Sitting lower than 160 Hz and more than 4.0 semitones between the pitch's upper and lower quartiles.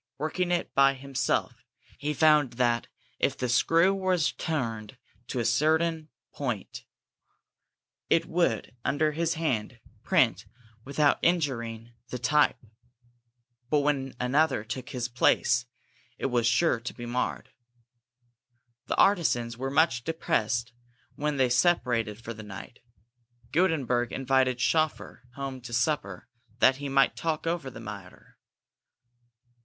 Yes: low, 135 Hz; average, 4.5 semitones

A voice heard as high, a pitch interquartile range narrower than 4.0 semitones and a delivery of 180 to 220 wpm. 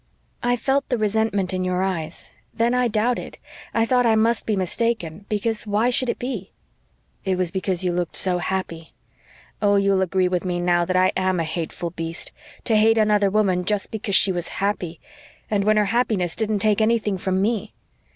Yes: high, 200 Hz; average, 3.3 semitones; average, 190 wpm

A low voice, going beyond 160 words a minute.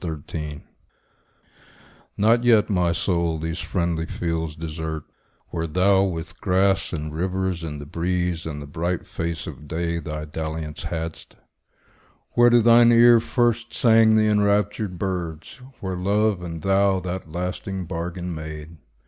No: very low, 90 Hz; average, 140 wpm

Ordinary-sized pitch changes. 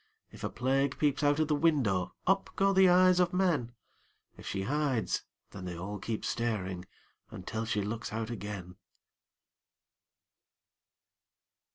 No: wide, 7.2 semitones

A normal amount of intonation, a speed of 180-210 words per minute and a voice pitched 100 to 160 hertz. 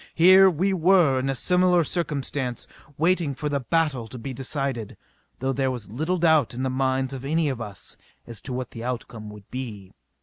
Yes: average, 4.7 semitones; average, 195 wpm; low, 135 Hz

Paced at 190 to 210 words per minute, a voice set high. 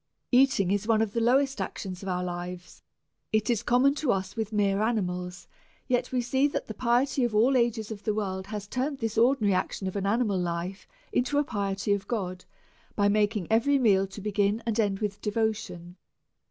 Yes: average, 200 wpm; high, 210 Hz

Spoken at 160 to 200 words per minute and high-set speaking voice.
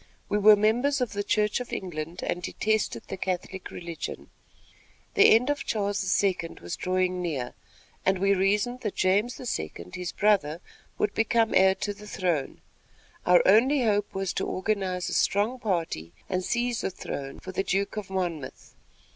Yes: average, 165 wpm; high, 195 Hz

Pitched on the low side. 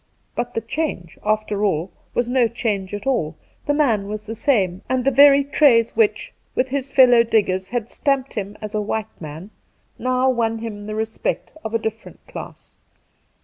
No: high, 225 Hz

